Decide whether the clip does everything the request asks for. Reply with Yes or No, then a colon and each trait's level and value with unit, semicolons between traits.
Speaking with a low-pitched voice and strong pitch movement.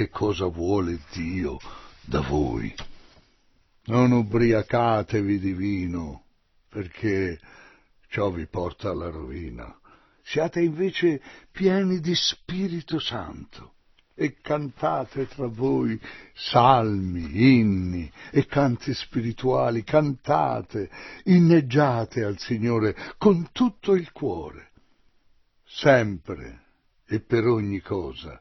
Yes: low, 115 Hz; wide, 7.1 semitones